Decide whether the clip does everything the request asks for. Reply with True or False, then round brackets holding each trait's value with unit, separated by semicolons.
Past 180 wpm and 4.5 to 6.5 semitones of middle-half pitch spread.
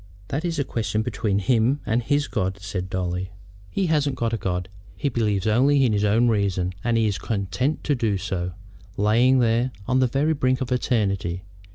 True (190 wpm; 4.8 semitones)